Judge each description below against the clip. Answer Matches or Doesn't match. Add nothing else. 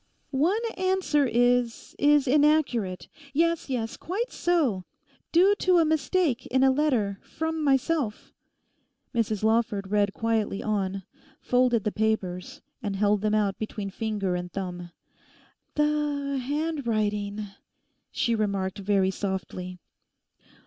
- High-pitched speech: Matches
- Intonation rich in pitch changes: Matches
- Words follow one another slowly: Matches